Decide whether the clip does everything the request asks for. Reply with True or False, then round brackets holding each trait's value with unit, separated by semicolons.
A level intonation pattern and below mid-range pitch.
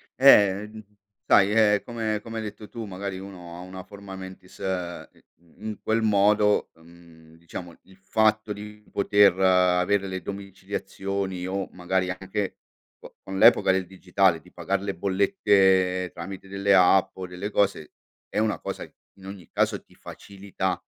True (1.9 semitones; 95 Hz)